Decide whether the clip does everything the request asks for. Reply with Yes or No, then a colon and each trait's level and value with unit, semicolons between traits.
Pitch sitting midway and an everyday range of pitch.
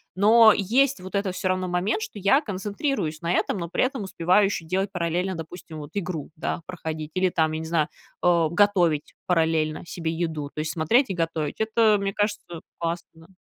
Yes: medium, 180 Hz; average, 3.9 semitones